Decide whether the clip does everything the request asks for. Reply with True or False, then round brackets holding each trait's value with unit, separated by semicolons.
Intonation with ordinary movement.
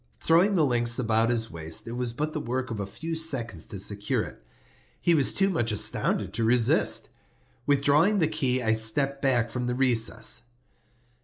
True (4.6 semitones)